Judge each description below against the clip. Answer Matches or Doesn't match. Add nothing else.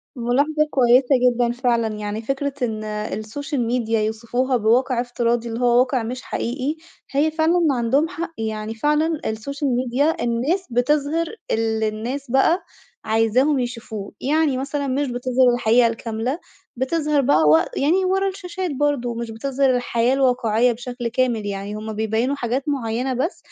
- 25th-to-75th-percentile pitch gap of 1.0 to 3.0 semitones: Doesn't match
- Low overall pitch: Doesn't match